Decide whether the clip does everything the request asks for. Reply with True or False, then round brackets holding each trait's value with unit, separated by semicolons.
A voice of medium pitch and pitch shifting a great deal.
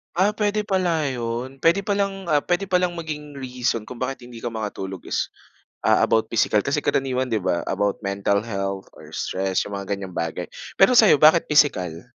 False (130 Hz; 8.9 semitones)